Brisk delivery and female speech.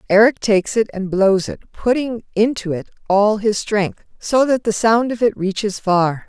No: average, 190 wpm; female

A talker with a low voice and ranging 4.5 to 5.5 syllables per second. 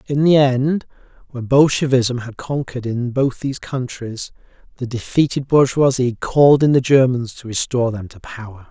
Yes: low, 130 Hz; 5.0 syllables/s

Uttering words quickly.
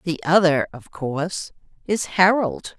No: slow, 130 wpm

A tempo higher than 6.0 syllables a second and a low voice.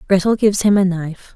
No: 6.8 syllables/s; high, 190 Hz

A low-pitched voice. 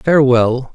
Yes: low, 130 Hz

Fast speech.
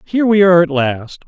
Yes: fast, 235 wpm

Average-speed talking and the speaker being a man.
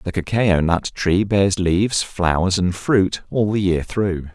Yes: average, 180 wpm; male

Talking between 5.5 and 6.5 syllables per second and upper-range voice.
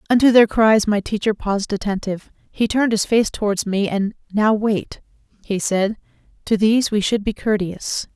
No: 5.1 syllables/s; high, 210 Hz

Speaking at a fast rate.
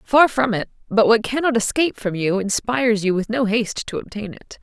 Yes: fast, 220 wpm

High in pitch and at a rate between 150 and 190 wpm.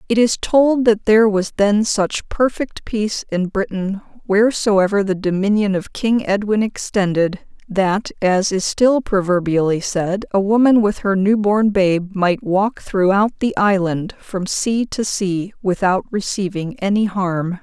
Yes: high, 200 Hz; average, 155 wpm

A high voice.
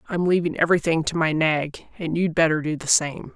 No: medium, 160 Hz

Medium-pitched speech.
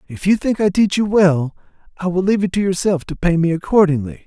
Yes: medium, 180 Hz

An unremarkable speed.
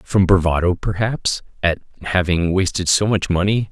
Yes: average, 145 wpm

